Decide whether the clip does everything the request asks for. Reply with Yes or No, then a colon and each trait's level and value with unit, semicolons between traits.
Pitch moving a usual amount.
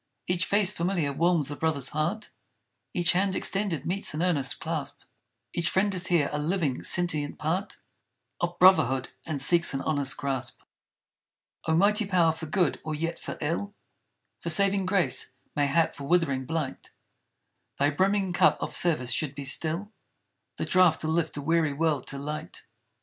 Yes: average, 3.9 semitones